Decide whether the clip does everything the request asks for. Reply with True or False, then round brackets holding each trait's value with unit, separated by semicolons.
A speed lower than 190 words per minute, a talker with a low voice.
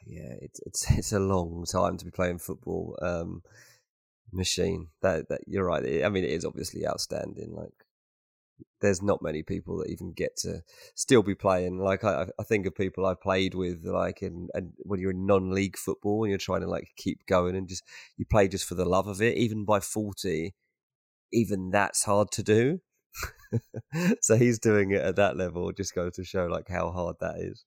False (205 wpm; 95 Hz)